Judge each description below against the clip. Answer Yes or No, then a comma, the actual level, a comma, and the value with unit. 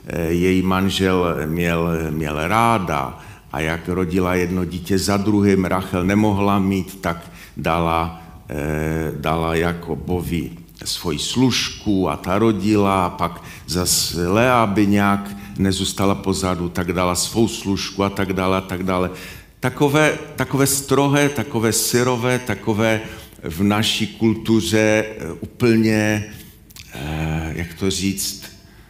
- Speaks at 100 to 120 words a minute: Yes, slow, 115 wpm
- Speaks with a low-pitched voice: Yes, very low, 95 Hz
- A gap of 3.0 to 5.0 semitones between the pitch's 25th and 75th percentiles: Yes, average, 3.9 semitones